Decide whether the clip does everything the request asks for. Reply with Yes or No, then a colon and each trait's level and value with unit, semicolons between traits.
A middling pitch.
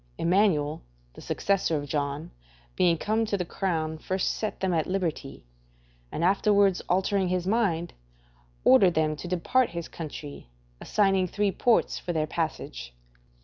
Yes: medium, 175 Hz